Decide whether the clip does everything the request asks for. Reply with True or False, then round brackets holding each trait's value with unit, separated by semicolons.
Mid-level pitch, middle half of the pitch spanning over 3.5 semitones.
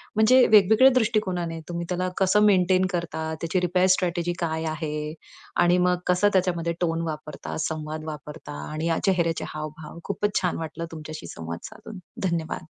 False (170 Hz; 2.7 semitones)